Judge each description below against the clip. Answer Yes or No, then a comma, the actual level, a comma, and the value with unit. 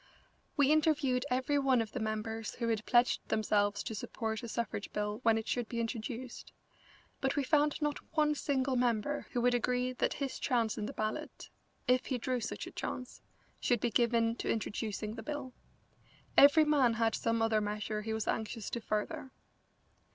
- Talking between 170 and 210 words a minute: Yes, average, 180 wpm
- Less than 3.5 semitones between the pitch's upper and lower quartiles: Yes, average, 3.0 semitones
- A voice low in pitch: No, high, 235 Hz